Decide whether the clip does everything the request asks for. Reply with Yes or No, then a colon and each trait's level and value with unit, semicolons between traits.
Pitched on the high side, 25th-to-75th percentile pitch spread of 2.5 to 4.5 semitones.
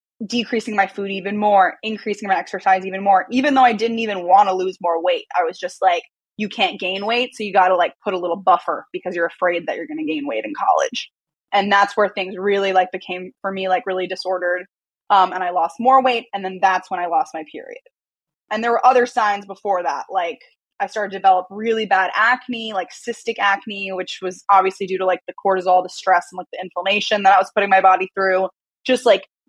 Yes: high, 195 Hz; average, 3.0 semitones